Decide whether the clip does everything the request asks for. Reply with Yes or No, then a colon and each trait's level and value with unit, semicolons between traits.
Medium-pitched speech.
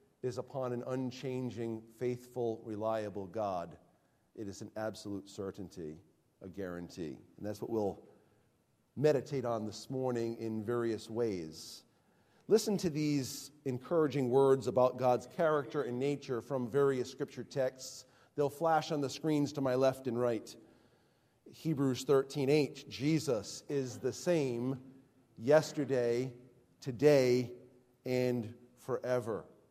No: low, 125 Hz